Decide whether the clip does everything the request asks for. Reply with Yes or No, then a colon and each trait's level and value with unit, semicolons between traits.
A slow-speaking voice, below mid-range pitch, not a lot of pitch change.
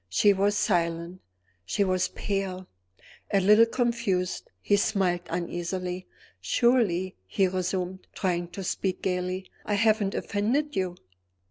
No: slow, 120 wpm; high, 190 Hz; narrow, 2.2 semitones